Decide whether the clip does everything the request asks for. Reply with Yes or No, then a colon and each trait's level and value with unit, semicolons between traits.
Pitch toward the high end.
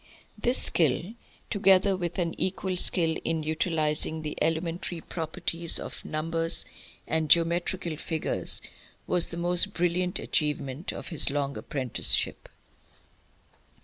No: medium, 165 Hz